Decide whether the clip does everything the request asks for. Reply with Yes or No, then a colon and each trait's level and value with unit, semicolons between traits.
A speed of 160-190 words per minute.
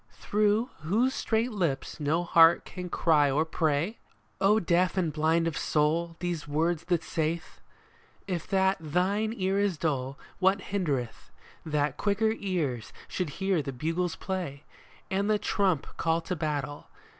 No: average, 150 wpm